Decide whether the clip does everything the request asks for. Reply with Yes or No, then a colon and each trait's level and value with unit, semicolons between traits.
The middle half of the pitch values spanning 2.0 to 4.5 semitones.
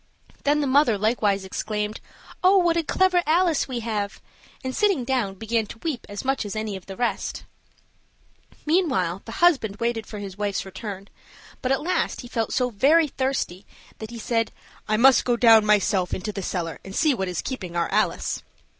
No: average, 5.2 semitones